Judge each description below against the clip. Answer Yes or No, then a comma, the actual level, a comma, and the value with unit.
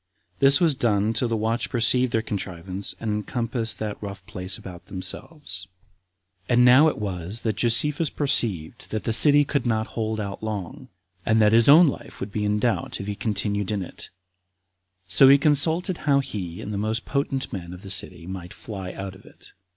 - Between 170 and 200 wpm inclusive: Yes, average, 195 wpm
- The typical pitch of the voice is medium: No, low, 110 Hz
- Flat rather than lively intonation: No, average, 4.6 semitones